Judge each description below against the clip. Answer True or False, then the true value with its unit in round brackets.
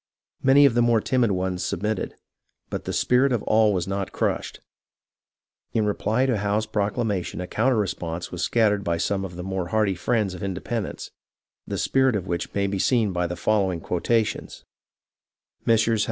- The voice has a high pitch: False (105 Hz)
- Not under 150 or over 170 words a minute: False (180 wpm)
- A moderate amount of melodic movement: True (3.7 semitones)